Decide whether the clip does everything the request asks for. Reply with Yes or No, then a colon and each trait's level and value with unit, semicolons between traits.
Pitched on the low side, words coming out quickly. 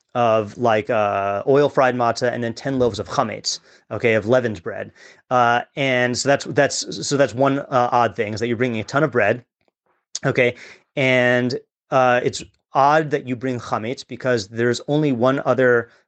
No: low, 125 Hz; average, 185 wpm